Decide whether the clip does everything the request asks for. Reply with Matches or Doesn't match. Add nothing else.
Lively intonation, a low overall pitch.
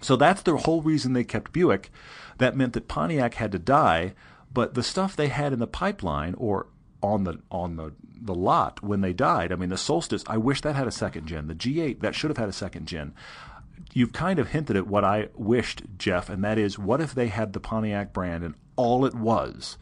Matches